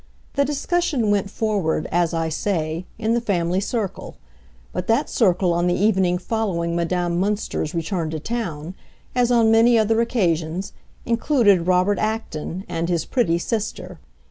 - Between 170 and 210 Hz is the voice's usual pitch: Yes, high, 190 Hz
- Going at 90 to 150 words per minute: Yes, average, 145 wpm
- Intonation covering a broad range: No, average, 4.7 semitones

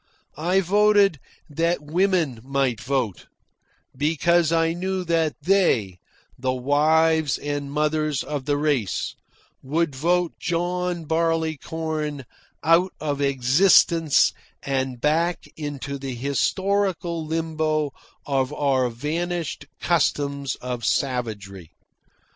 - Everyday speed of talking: No, slow, 100 wpm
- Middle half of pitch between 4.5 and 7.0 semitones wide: No, average, 3.5 semitones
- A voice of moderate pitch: Yes, medium, 150 Hz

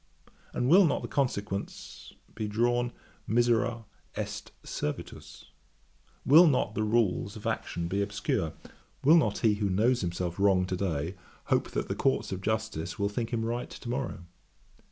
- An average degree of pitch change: Yes, average, 3.7 semitones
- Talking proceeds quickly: No, average, 160 wpm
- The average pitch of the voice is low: Yes, low, 110 Hz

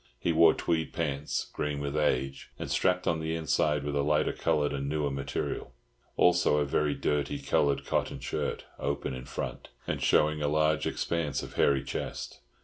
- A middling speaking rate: Yes, average, 175 wpm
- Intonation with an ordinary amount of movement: No, narrow, 1.8 semitones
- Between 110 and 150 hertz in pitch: No, very low, 75 Hz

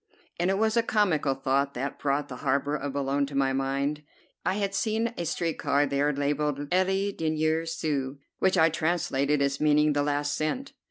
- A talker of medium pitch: Yes, medium, 150 Hz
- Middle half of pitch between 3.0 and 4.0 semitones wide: Yes, average, 3.7 semitones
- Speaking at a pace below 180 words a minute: No, average, 185 wpm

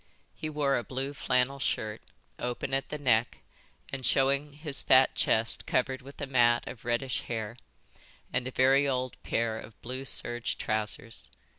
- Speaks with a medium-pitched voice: No, low, 130 Hz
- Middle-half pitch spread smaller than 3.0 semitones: Yes, narrow, 2.5 semitones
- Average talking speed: Yes, average, 160 wpm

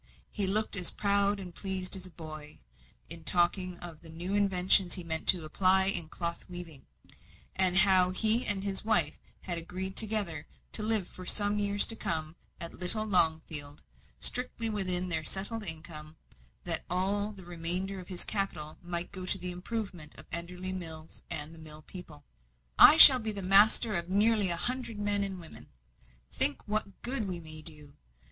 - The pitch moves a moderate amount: Yes, average, 3.2 semitones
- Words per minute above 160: Yes, average, 170 wpm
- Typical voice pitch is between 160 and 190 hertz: Yes, medium, 185 Hz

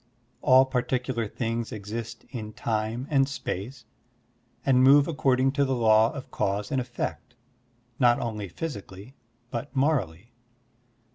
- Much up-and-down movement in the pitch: No, average, 3.5 semitones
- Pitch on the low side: Yes, low, 120 Hz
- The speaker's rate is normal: No, slow, 125 wpm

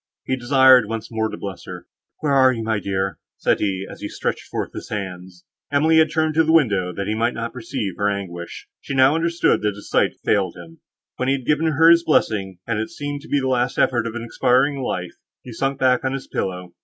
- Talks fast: Yes, fast, 235 wpm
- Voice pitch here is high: No, low, 120 Hz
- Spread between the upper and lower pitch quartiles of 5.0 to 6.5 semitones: Yes, wide, 5.6 semitones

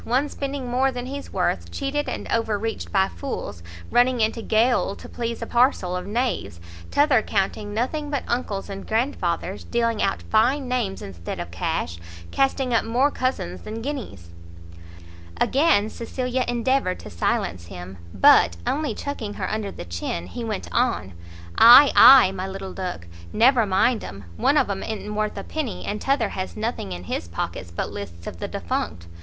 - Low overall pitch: No, high, 220 Hz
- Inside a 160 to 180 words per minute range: Yes, average, 175 wpm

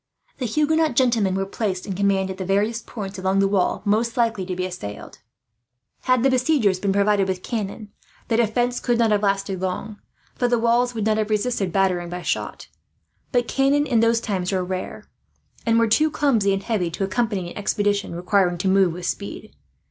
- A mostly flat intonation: No, average, 3.6 semitones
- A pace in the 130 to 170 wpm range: No, average, 195 wpm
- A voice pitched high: Yes, high, 205 Hz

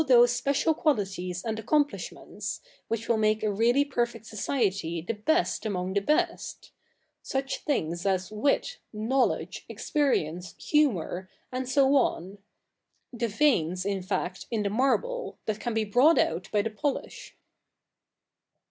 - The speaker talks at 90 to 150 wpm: Yes, average, 140 wpm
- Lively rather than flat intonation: Yes, wide, 5.8 semitones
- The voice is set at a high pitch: Yes, high, 225 Hz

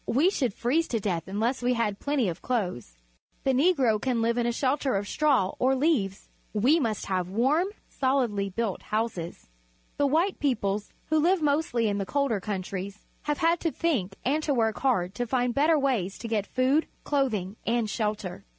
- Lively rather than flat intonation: Yes, wide, 5.7 semitones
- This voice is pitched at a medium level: No, high, 240 Hz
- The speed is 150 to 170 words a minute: No, average, 185 wpm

